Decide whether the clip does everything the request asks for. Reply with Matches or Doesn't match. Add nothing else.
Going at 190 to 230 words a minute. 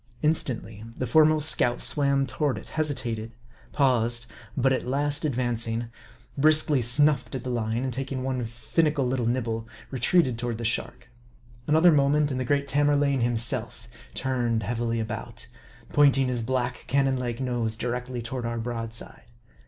Doesn't match